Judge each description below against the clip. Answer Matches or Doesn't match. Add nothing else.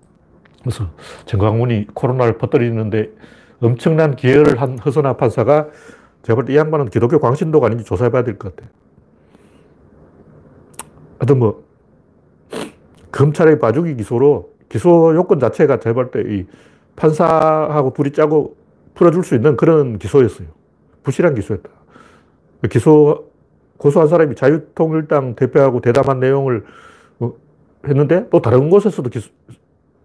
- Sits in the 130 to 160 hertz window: Matches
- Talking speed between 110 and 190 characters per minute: Doesn't match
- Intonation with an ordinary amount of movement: Matches